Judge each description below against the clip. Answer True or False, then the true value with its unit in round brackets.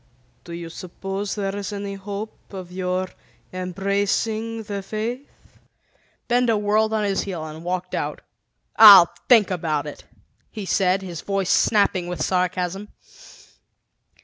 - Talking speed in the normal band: False (130 wpm)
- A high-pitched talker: True (195 Hz)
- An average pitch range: False (2.3 semitones)